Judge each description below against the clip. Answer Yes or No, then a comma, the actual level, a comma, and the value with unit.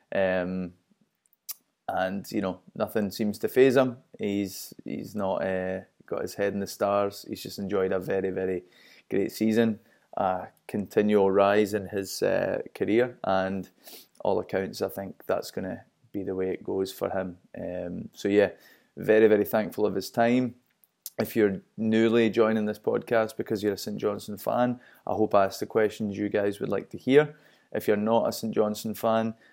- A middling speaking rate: Yes, average, 180 wpm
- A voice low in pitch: Yes, low, 105 Hz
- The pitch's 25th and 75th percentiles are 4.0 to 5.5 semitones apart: No, average, 2.7 semitones